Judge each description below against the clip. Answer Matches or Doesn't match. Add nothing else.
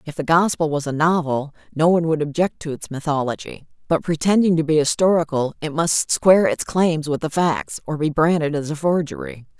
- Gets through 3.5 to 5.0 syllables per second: Doesn't match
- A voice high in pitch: Doesn't match